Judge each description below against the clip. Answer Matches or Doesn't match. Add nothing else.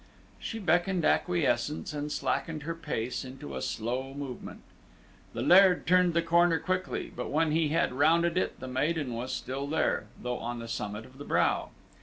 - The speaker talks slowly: Doesn't match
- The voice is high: Doesn't match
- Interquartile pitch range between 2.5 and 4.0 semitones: Doesn't match